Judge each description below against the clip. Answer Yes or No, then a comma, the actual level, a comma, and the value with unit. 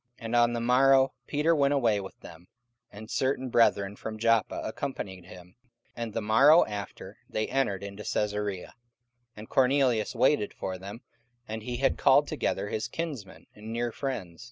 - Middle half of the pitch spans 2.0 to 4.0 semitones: No, average, 4.4 semitones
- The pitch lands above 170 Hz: No, low, 115 Hz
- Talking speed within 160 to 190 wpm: Yes, average, 165 wpm